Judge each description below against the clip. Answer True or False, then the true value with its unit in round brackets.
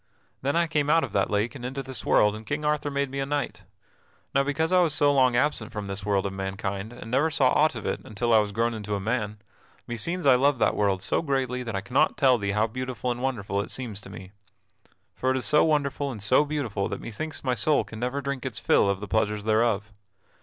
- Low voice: True (120 Hz)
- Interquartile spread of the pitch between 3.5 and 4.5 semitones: False (4.9 semitones)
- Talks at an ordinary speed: False (245 wpm)